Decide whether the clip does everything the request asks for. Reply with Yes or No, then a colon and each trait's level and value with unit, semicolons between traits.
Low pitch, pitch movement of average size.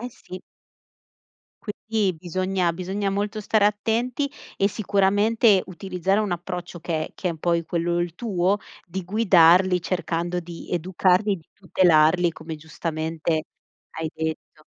No: medium, 180 Hz; average, 3.1 semitones